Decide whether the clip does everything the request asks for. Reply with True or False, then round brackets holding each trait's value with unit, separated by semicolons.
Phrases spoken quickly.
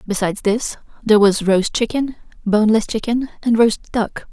False (155 wpm)